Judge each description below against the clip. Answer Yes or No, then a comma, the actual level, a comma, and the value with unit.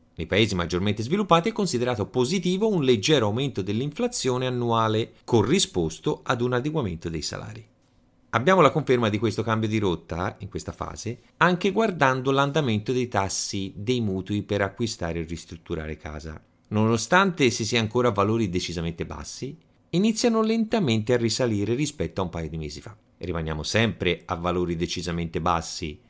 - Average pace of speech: Yes, average, 155 wpm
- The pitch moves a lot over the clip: Yes, wide, 6.2 semitones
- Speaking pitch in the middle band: No, low, 110 Hz